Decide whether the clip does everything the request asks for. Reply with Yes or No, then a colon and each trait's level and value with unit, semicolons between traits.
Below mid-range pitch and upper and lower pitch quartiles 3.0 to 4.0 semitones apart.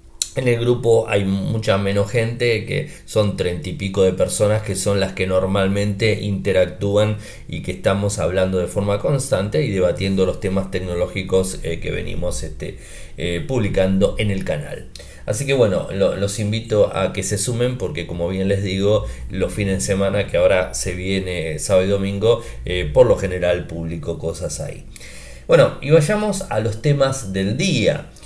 No: low, 100 Hz; narrow, 2.5 semitones